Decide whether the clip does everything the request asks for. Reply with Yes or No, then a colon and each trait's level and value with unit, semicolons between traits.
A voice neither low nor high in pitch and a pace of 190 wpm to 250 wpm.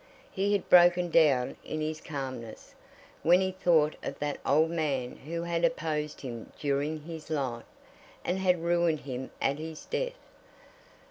No: medium, 155 Hz; average, 150 wpm